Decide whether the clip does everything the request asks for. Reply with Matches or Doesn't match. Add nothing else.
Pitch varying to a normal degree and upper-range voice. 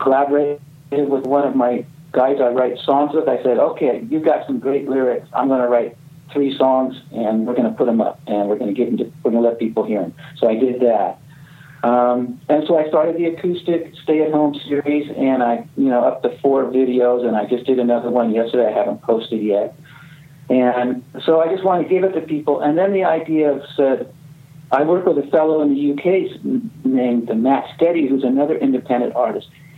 Doesn't match